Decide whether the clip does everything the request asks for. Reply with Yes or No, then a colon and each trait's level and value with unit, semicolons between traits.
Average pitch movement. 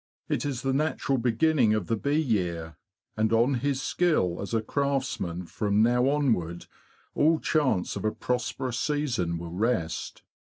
No: wide, 5.9 semitones